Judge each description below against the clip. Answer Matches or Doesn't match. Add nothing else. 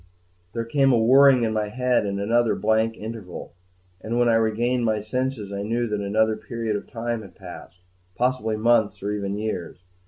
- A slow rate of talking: Doesn't match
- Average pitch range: Doesn't match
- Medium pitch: Doesn't match